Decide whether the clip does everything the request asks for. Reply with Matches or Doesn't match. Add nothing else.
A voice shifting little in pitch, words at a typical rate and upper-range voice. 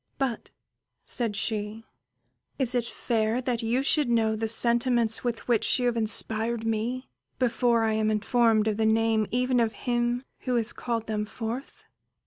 Matches